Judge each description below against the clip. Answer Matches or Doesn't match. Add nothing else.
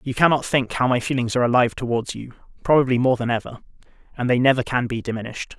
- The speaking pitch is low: Matches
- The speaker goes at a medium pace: Doesn't match